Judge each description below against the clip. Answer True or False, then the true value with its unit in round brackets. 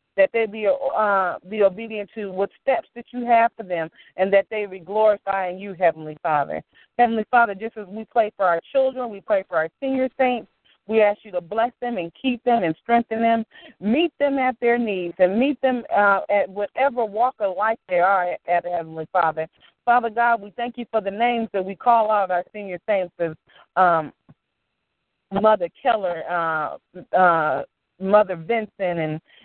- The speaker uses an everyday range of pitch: True (4.6 semitones)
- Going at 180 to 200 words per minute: True (185 wpm)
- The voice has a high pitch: True (210 Hz)